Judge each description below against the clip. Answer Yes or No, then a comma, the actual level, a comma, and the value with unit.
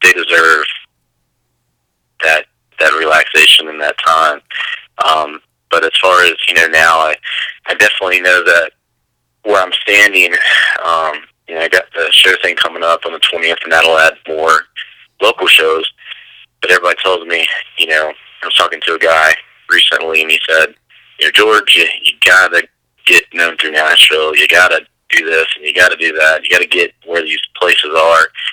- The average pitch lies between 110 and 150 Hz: No, very low, 80 Hz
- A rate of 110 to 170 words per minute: No, average, 180 wpm